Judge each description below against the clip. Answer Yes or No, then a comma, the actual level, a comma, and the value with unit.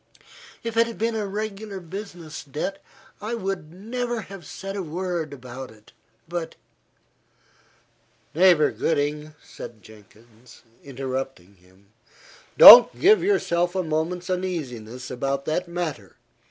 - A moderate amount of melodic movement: No, wide, 6.6 semitones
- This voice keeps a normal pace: No, slow, 120 wpm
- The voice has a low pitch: No, medium, 170 Hz